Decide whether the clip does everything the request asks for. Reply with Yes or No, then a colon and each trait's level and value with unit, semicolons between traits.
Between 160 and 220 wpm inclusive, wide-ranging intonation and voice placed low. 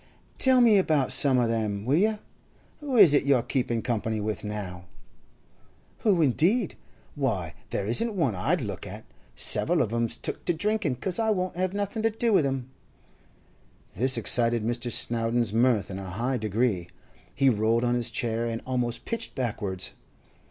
Yes: average, 170 wpm; wide, 7.6 semitones; low, 120 Hz